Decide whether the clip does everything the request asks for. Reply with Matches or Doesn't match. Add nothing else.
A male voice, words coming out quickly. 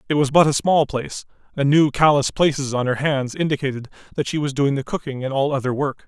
Matches